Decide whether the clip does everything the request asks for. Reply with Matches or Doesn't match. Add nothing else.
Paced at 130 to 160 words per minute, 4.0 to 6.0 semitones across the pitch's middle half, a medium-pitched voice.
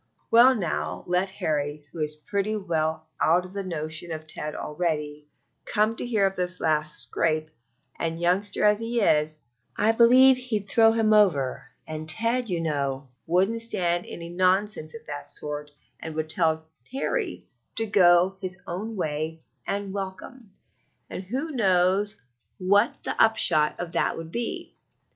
Matches